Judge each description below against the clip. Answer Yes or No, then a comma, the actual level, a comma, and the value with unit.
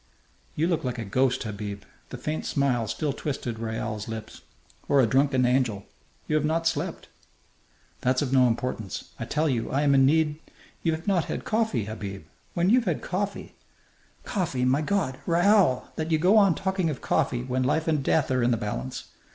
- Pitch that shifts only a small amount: No, average, 5.1 semitones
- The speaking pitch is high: No, low, 135 Hz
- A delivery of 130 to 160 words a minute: No, average, 190 wpm